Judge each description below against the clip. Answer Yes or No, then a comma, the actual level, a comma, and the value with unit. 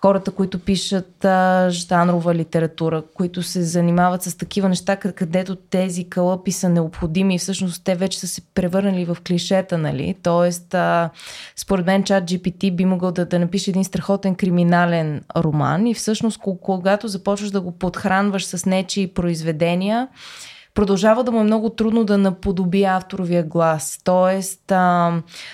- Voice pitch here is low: No, medium, 185 Hz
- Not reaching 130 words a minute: No, average, 150 wpm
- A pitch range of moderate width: No, narrow, 1.9 semitones